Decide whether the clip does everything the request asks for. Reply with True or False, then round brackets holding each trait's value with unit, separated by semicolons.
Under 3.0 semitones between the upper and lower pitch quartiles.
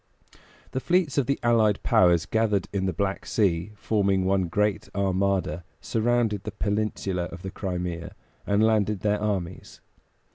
True (2.6 semitones)